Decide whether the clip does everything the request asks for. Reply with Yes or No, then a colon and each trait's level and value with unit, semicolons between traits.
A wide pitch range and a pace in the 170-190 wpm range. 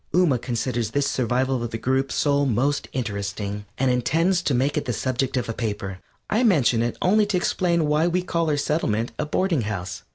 No: wide, 5.7 semitones; average, 200 wpm